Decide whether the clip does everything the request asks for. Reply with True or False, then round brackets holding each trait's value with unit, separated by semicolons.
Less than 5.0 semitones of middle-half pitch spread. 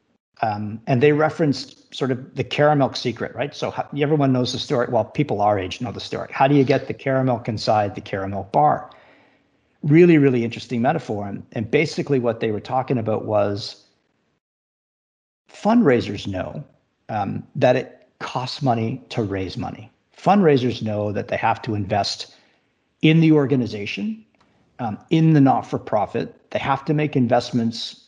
False (5.3 semitones)